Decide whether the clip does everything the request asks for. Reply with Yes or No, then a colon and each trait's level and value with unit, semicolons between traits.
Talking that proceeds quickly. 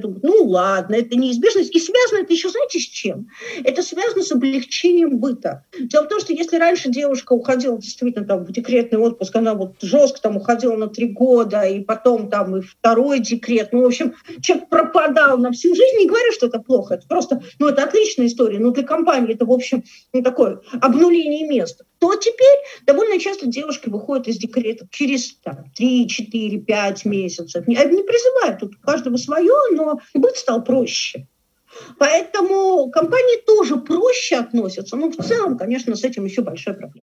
Yes: fast, 180 wpm